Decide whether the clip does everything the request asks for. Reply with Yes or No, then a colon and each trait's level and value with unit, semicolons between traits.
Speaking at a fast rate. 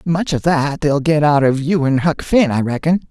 Yes: fast, 250 wpm